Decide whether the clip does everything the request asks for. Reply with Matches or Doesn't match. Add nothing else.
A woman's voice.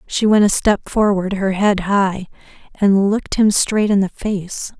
Matches